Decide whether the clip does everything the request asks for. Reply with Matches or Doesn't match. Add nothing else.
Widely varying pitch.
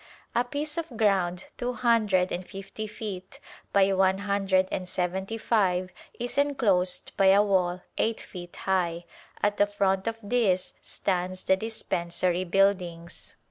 Doesn't match